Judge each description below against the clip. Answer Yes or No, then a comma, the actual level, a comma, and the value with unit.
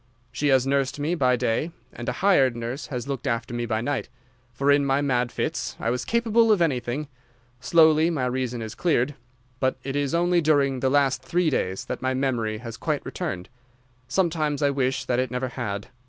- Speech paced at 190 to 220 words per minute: Yes, average, 200 wpm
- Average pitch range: Yes, average, 3.4 semitones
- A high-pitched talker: No, low, 135 Hz